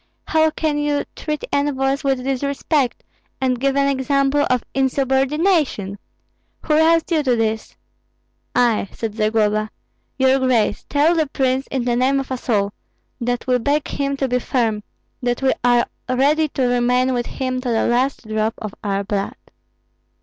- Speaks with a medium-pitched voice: No, very high, 260 Hz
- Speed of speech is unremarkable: Yes, average, 160 wpm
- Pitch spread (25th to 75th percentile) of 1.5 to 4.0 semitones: Yes, average, 2.7 semitones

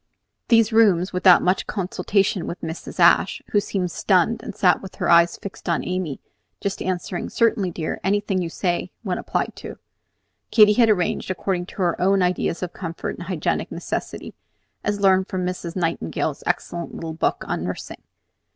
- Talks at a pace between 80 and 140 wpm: No, average, 170 wpm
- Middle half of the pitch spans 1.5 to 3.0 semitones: Yes, narrow, 2.4 semitones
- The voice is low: No, medium, 185 Hz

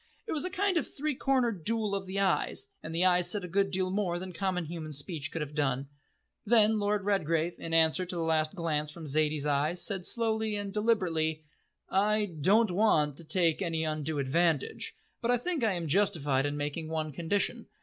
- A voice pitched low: No, medium, 175 Hz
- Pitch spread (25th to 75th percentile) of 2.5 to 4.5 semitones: No, average, 4.9 semitones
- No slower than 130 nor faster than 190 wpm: No, average, 200 wpm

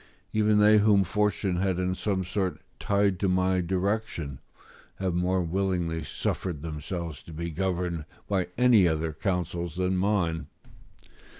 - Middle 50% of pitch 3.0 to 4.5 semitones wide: No, narrow, 2.6 semitones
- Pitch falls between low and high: No, very low, 90 Hz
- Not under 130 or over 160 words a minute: Yes, slow, 135 wpm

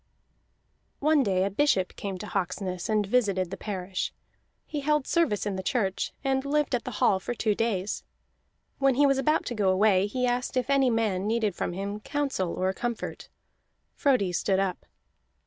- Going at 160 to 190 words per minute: Yes, average, 180 wpm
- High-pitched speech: Yes, high, 210 Hz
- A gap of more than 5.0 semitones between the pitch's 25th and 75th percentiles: Yes, wide, 5.6 semitones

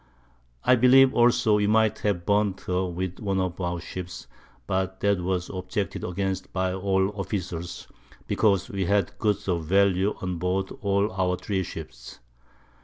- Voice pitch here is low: Yes, very low, 95 Hz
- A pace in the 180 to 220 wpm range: No, average, 160 wpm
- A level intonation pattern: Yes, narrow, 1.9 semitones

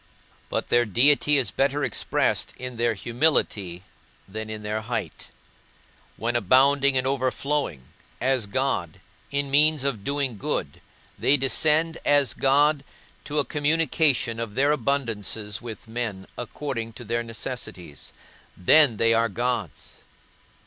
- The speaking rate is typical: No, slow, 130 wpm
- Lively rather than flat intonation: No, average, 4.1 semitones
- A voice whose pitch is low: Yes, low, 125 Hz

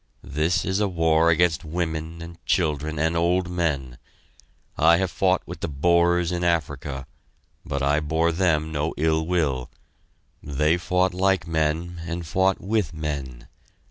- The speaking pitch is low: Yes, very low, 80 Hz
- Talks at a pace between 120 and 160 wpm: Yes, average, 145 wpm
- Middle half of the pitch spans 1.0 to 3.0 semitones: Yes, narrow, 2.5 semitones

